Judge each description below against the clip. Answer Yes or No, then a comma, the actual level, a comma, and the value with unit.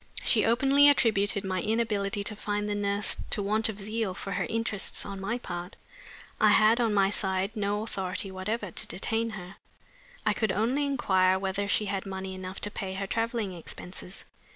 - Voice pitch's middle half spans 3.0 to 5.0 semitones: No, narrow, 2.5 semitones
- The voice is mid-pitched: No, high, 205 Hz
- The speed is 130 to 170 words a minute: No, average, 180 wpm